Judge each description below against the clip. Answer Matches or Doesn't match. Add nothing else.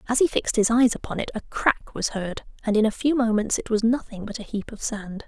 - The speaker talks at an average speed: Doesn't match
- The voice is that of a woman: Matches